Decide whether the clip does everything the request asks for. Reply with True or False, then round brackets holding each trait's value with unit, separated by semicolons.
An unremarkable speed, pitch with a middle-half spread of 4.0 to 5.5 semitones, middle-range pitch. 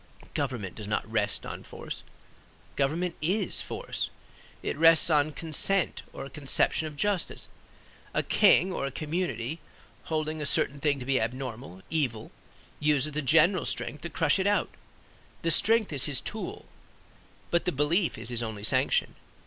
True (155 wpm; 4.5 semitones; 150 Hz)